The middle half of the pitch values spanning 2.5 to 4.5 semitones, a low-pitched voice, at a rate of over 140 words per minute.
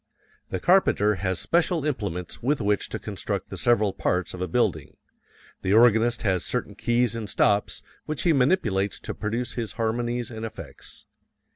Yes: average, 3.4 semitones; low, 115 Hz; average, 160 wpm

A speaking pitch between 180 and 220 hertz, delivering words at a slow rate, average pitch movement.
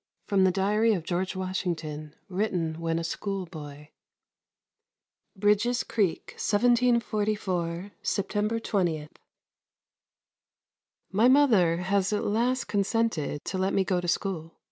Yes: high, 190 Hz; slow, 115 wpm; average, 3.9 semitones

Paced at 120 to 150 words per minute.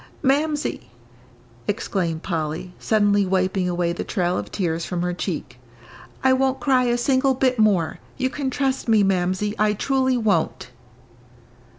Yes: average, 145 wpm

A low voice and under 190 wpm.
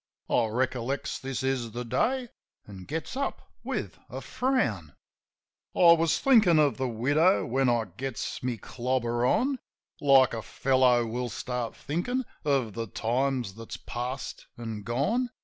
Yes: low, 130 Hz; average, 150 wpm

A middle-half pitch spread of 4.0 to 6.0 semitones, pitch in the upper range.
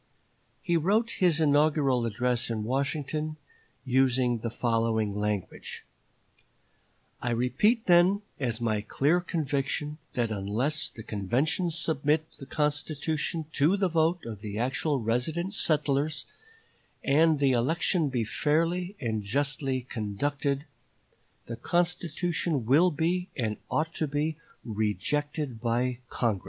No: average, 5.2 semitones; medium, 140 Hz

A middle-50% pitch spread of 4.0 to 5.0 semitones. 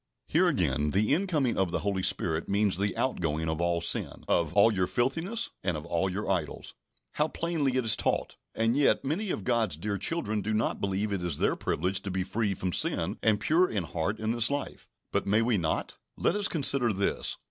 No: wide, 5.6 semitones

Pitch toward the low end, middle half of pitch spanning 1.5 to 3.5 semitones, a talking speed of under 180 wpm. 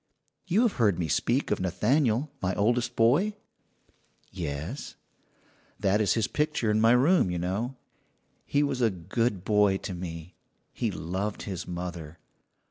No: low, 105 Hz; wide, 5.4 semitones; average, 145 wpm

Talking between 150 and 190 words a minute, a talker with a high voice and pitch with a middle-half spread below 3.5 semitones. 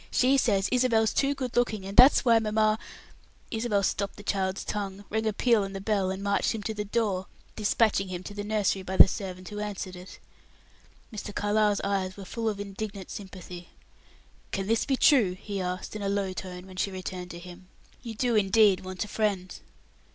No: fast, 205 wpm; high, 200 Hz; narrow, 2.4 semitones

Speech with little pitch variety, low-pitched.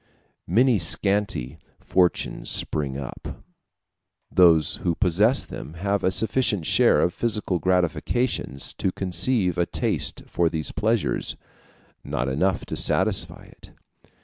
No: average, 4.3 semitones; very low, 90 Hz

